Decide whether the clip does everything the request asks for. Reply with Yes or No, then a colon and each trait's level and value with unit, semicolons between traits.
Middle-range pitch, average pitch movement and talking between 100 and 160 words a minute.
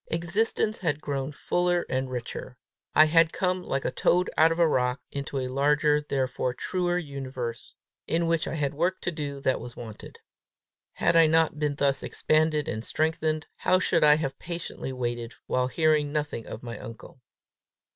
No: medium, 150 Hz; average, 4.0 semitones; average, 175 wpm